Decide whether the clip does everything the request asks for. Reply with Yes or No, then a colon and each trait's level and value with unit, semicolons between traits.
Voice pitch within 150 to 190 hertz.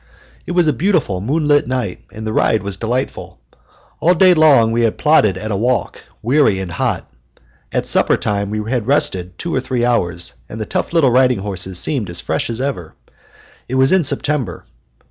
No: low, 120 Hz